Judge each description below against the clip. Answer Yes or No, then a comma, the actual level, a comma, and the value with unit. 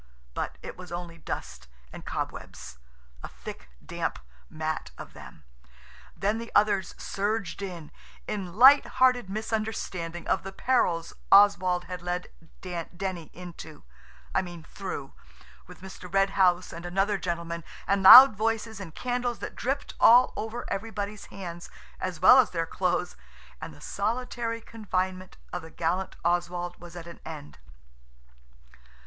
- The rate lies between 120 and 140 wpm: Yes, slow, 135 wpm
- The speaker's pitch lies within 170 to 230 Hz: Yes, medium, 185 Hz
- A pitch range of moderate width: Yes, average, 3.8 semitones